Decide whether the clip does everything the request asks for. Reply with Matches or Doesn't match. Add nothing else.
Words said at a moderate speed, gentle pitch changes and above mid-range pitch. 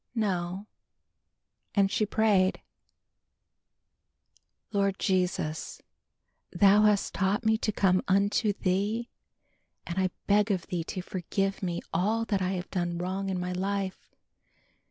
Doesn't match